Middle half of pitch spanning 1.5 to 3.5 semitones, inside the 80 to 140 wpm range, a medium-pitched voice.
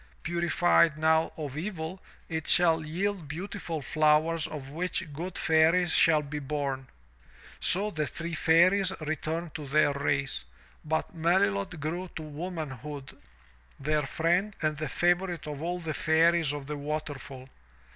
Yes: narrow, 2.6 semitones; slow, 135 wpm; medium, 160 Hz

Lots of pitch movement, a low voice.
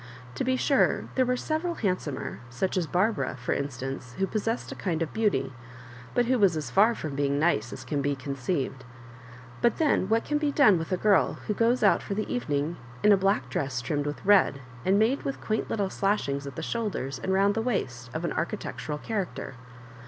No: wide, 7.8 semitones; medium, 185 Hz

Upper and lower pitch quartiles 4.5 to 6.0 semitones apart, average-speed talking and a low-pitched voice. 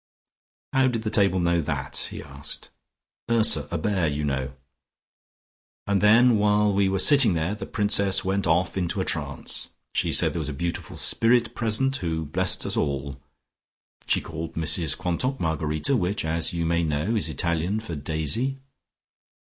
Yes: average, 4.9 semitones; average, 165 wpm; very low, 90 Hz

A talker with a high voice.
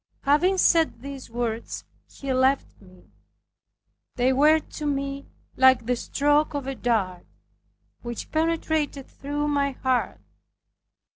Yes: very high, 275 Hz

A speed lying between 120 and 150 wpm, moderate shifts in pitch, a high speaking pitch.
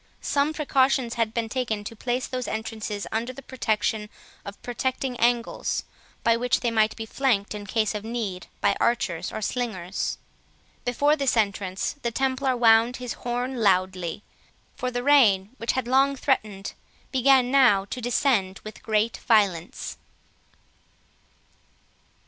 Yes: average, 140 wpm; average, 3.5 semitones; high, 230 Hz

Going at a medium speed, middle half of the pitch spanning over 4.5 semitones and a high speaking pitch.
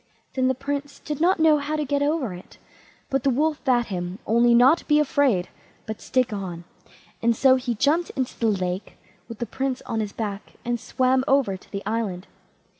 Yes: average, 195 wpm; average, 5.1 semitones; very high, 250 Hz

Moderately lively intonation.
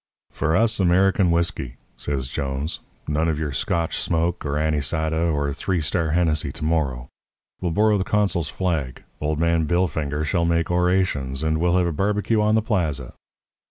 Yes: average, 3.1 semitones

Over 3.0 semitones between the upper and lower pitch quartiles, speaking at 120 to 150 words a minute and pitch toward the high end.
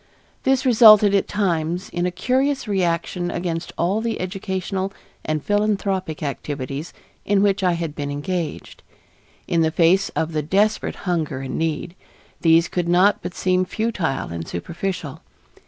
No: average, 3.7 semitones; average, 145 wpm; medium, 180 Hz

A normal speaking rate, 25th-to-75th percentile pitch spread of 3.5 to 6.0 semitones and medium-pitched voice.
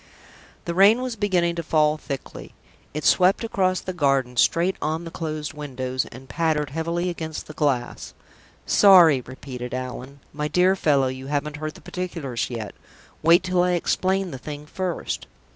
Yes: average, 160 wpm; average, 4.6 semitones; medium, 155 Hz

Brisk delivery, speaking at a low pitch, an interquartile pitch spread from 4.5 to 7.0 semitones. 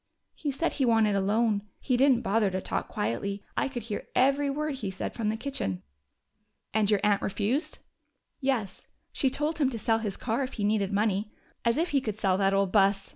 No: fast, 210 wpm; high, 220 Hz; average, 4.9 semitones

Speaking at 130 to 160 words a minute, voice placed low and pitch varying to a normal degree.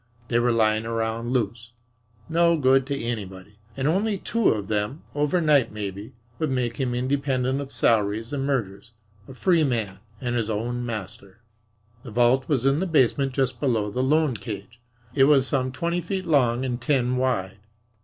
No: average, 170 wpm; low, 125 Hz; average, 3.8 semitones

